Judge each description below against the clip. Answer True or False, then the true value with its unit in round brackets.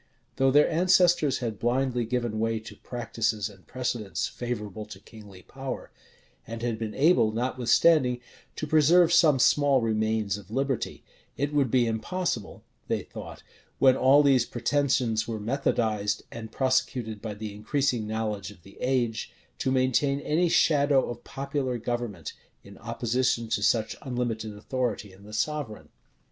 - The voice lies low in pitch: True (120 Hz)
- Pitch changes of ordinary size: True (3.7 semitones)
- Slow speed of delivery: False (145 wpm)